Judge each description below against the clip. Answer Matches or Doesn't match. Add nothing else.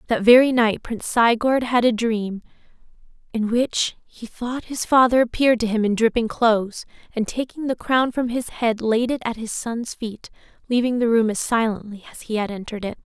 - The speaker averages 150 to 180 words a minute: Doesn't match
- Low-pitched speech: Doesn't match